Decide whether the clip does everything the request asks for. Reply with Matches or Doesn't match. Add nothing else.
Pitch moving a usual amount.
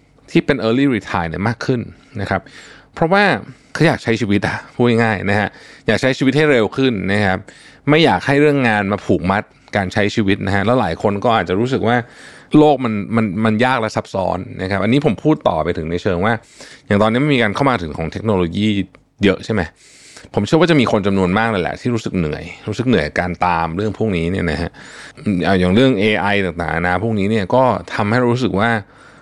Matches